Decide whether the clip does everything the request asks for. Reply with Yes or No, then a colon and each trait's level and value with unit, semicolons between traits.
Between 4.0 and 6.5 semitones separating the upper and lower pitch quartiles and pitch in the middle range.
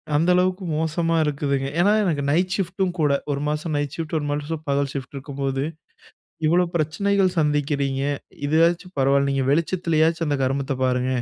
No: average, 3.3 semitones; medium, 150 Hz